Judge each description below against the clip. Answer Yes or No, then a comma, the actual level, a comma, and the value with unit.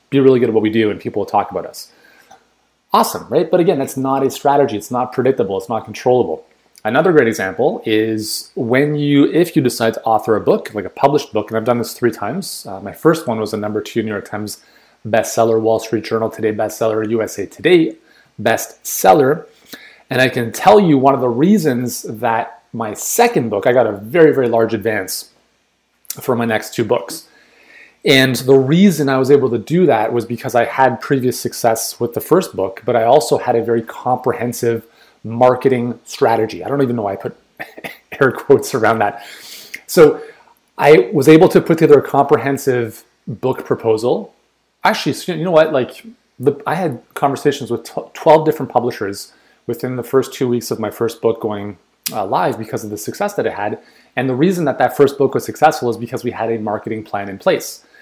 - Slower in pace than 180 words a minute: No, average, 200 wpm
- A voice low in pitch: Yes, low, 125 Hz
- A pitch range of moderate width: Yes, average, 3.9 semitones